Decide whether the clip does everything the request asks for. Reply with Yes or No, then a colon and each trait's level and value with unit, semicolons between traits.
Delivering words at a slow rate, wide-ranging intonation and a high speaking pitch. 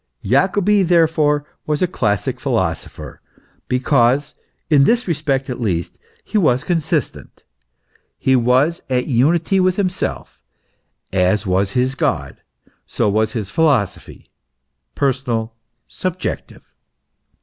No: slow, 110 wpm; wide, 6.4 semitones; low, 135 Hz